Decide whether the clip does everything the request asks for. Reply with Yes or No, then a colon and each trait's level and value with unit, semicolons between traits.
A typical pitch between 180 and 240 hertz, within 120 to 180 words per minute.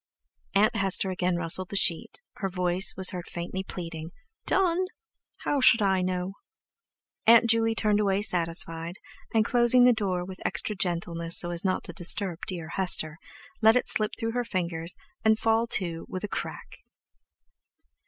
Yes: high, 190 Hz; average, 160 wpm